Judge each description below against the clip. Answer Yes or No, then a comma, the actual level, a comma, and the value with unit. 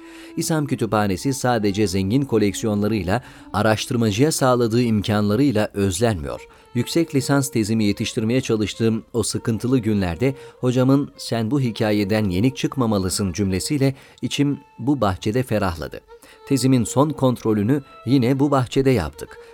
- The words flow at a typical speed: Yes, average, 110 wpm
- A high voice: No, low, 120 Hz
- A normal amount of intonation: Yes, average, 4.4 semitones